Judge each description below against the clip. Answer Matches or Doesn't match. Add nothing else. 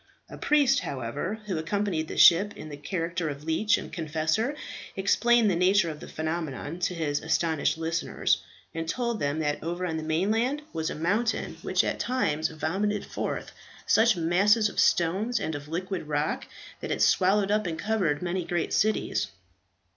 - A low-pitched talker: Doesn't match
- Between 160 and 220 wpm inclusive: Matches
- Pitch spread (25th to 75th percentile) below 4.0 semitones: Doesn't match